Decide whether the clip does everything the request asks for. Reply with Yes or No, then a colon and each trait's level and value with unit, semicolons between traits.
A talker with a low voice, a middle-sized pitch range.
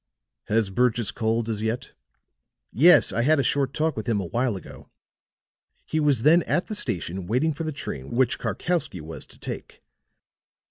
No: low, 120 Hz; wide, 5.7 semitones